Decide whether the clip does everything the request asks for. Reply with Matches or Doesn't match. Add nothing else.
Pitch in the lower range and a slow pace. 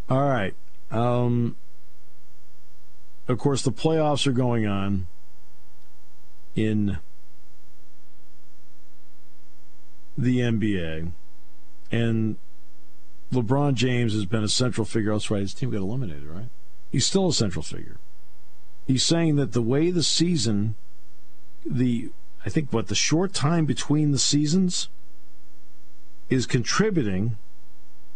Matches